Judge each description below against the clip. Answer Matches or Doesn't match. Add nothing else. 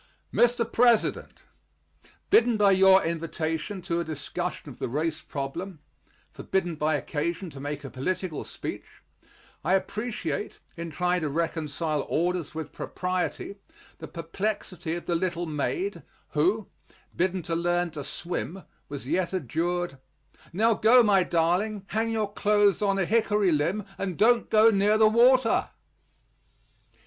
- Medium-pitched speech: Matches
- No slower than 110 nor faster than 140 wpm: Matches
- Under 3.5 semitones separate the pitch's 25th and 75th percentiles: Doesn't match